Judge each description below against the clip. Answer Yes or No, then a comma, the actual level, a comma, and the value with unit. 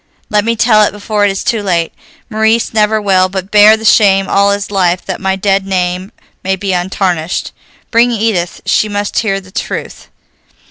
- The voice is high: Yes, high, 200 Hz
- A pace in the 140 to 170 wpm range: No, average, 185 wpm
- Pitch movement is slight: Yes, narrow, 2.2 semitones